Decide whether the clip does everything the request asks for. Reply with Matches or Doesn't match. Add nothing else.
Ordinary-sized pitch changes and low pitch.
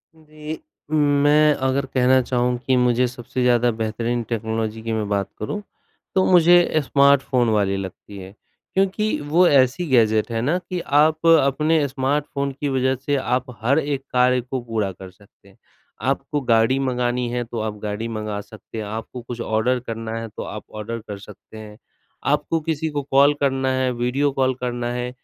Matches